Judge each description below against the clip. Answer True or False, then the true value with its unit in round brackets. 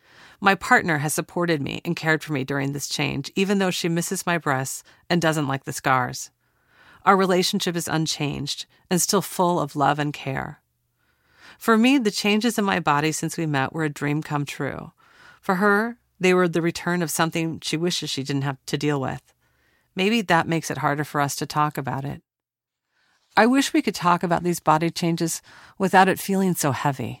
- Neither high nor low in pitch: True (165 Hz)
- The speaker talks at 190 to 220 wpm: True (200 wpm)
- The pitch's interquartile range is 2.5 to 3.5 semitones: False (4.2 semitones)